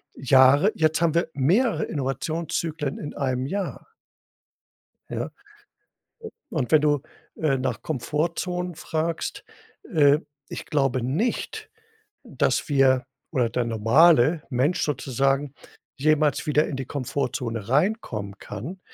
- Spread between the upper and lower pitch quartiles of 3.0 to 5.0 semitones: Yes, average, 3.6 semitones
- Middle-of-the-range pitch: Yes, medium, 145 Hz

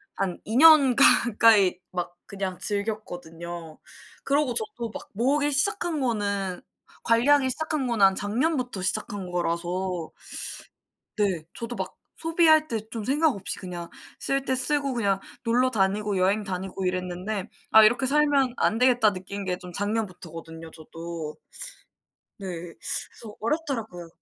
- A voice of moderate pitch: No, high, 210 Hz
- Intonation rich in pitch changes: Yes, wide, 6.1 semitones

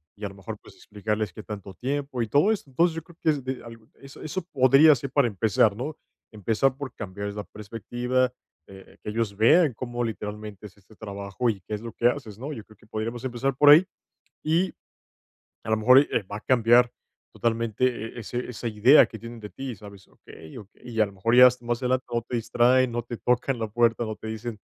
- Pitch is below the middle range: Yes, low, 115 Hz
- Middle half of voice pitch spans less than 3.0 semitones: No, average, 3.3 semitones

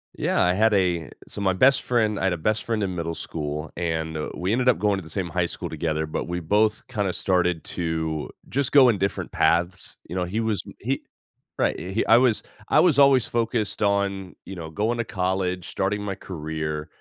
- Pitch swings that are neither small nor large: Yes, average, 4.3 semitones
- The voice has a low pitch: Yes, very low, 95 Hz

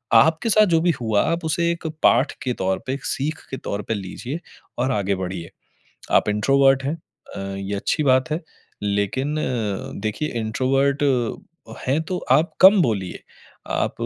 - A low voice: Yes, low, 130 Hz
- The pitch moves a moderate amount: No, wide, 6.9 semitones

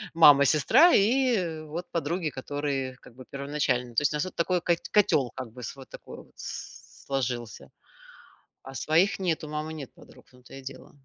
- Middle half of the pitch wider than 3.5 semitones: Yes, average, 4.2 semitones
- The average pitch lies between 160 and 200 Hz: No, medium, 145 Hz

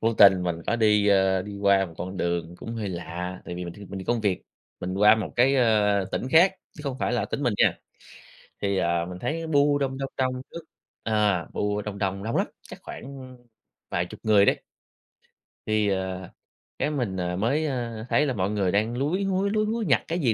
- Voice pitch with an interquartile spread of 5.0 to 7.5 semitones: Yes, wide, 5.6 semitones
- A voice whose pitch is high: No, low, 105 Hz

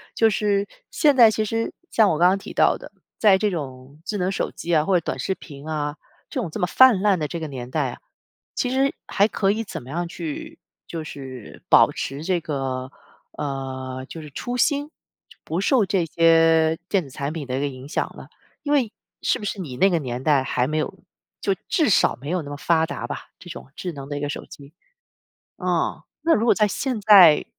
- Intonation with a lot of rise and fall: Yes, wide, 6.4 semitones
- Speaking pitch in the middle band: Yes, medium, 170 Hz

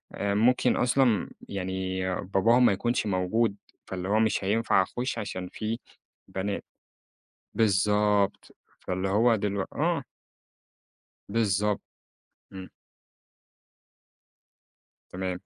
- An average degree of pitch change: Yes, average, 3.0 semitones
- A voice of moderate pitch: No, low, 100 Hz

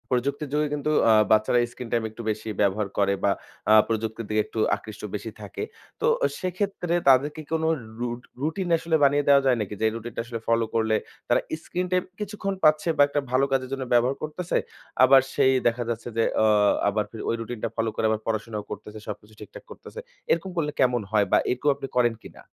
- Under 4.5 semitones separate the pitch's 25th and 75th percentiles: No, average, 5.3 semitones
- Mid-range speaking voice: No, low, 125 Hz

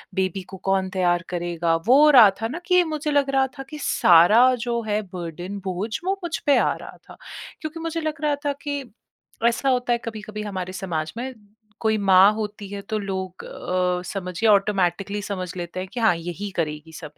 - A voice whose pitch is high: Yes, high, 200 Hz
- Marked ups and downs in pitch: Yes, wide, 5.7 semitones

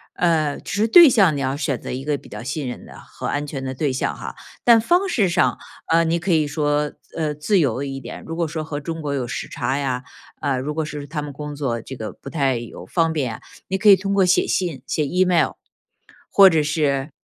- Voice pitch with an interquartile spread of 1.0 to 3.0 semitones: No, average, 3.7 semitones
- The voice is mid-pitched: Yes, medium, 150 Hz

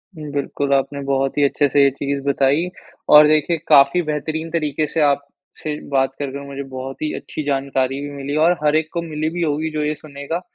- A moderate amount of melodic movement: No, narrow, 1.9 semitones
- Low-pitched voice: No, medium, 145 Hz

